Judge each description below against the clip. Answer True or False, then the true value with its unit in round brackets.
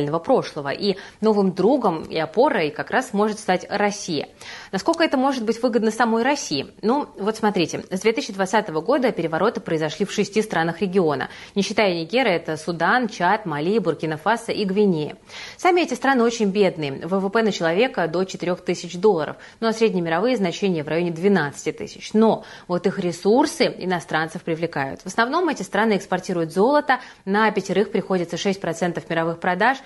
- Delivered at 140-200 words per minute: True (160 wpm)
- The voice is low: False (200 Hz)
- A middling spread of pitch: True (4.7 semitones)